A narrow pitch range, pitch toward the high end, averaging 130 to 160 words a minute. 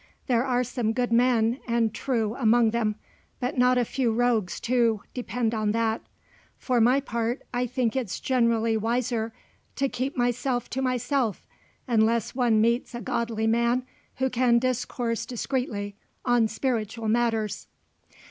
Yes: narrow, 1.9 semitones; high, 235 Hz; average, 145 wpm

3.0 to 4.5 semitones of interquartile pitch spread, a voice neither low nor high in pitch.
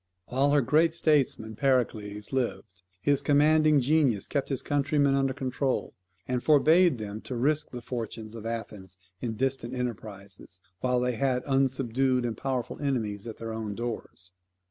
No: average, 3.9 semitones; low, 125 Hz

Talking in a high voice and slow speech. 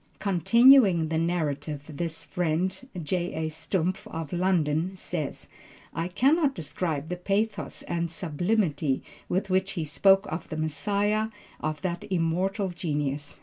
No: medium, 175 Hz; slow, 125 wpm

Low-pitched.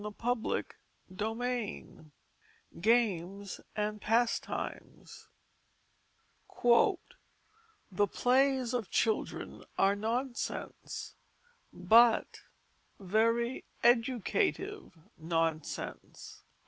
No: high, 230 Hz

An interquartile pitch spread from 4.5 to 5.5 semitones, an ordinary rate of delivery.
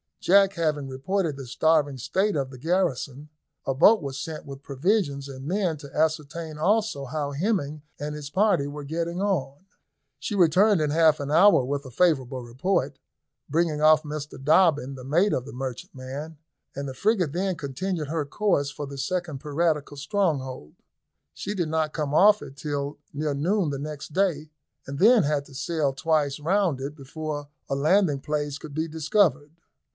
No: average, 3.7 semitones; average, 170 wpm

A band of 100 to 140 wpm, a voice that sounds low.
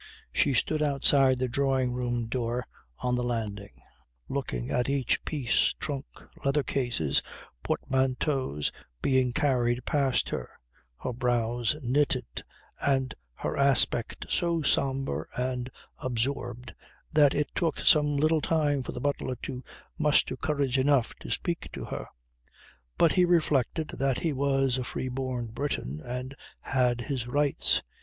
Yes: slow, 135 wpm; low, 130 Hz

